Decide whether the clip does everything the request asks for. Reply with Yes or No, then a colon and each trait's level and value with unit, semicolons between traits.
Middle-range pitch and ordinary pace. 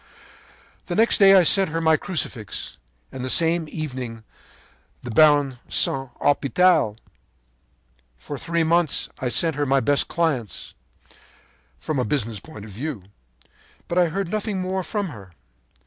Yes: medium, 155 Hz; average, 150 wpm